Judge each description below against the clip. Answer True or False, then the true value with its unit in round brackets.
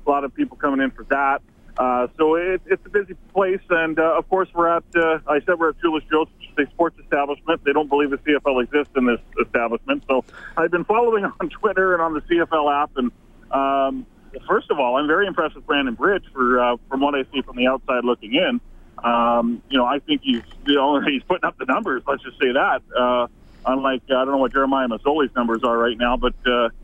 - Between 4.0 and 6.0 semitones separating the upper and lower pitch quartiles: True (4.6 semitones)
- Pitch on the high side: False (140 Hz)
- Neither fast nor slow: False (230 wpm)